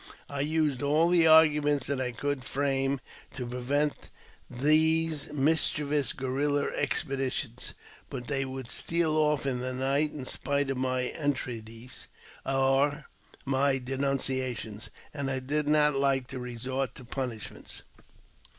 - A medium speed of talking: No, slow, 130 wpm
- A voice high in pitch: No, low, 135 Hz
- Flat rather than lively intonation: Yes, narrow, 2.2 semitones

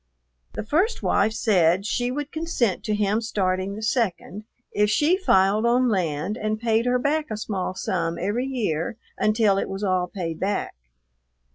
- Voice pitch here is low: No, high, 210 Hz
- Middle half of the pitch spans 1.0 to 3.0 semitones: No, average, 4.2 semitones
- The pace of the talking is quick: No, average, 165 wpm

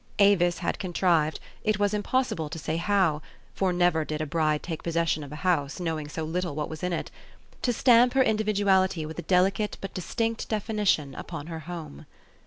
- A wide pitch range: No, average, 4.4 semitones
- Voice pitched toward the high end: No, medium, 175 Hz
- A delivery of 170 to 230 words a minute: Yes, average, 190 wpm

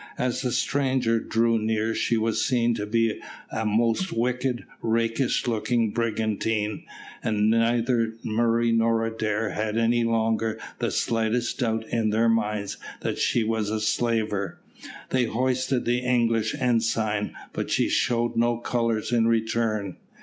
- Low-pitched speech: Yes, low, 115 Hz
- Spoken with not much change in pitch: Yes, narrow, 1.3 semitones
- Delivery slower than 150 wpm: Yes, average, 140 wpm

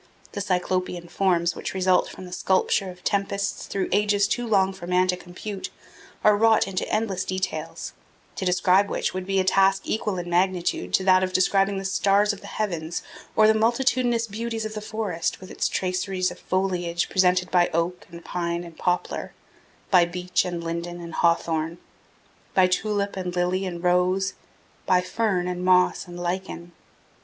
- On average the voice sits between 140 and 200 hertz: Yes, medium, 185 Hz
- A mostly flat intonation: Yes, narrow, 1.9 semitones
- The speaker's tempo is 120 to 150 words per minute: No, average, 175 wpm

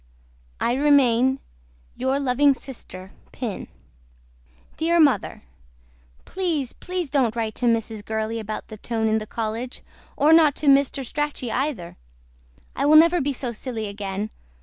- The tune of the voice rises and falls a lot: No, average, 4.6 semitones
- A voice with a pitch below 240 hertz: No, very high, 255 Hz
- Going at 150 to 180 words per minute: No, average, 140 wpm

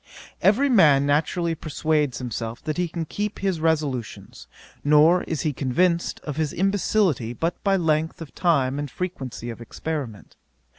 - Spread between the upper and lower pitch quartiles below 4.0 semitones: No, average, 4.3 semitones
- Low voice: No, medium, 155 Hz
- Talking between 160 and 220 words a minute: No, average, 150 wpm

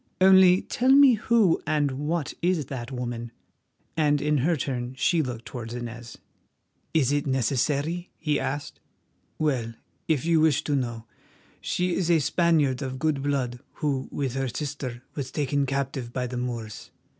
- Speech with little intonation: No, average, 4.1 semitones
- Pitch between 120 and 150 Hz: Yes, medium, 140 Hz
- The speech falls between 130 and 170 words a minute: Yes, average, 155 wpm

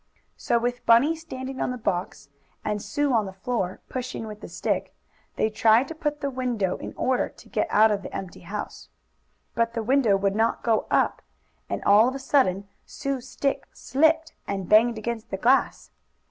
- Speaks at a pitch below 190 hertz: No, high, 235 Hz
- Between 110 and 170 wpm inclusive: No, average, 190 wpm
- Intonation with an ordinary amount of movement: Yes, average, 4.1 semitones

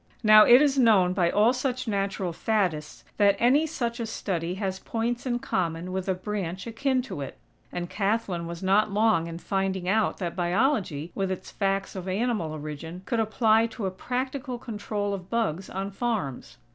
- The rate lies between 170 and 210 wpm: Yes, average, 180 wpm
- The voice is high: Yes, high, 200 Hz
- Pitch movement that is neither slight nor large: Yes, average, 4.2 semitones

